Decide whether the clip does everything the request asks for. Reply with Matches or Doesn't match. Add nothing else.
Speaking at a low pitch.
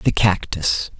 Matches